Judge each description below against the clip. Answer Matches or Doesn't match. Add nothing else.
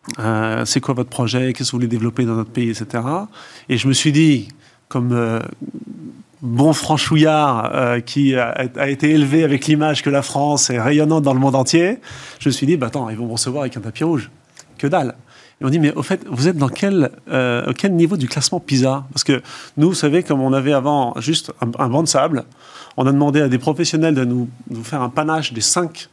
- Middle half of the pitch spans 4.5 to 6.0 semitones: Doesn't match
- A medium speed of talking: Doesn't match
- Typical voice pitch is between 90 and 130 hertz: Doesn't match